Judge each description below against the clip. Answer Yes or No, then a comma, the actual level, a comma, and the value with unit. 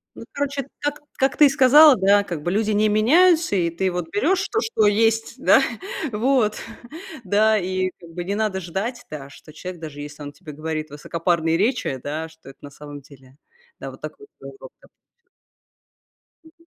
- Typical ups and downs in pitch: No, wide, 7.5 semitones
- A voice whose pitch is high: Yes, high, 195 Hz